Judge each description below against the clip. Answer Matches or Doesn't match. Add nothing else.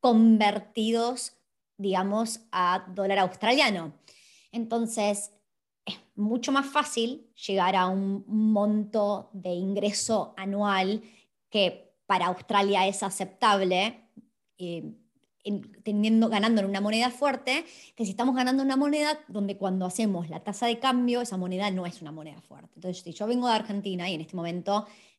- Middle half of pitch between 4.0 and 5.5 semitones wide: Doesn't match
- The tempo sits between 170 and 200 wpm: Doesn't match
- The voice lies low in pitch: Doesn't match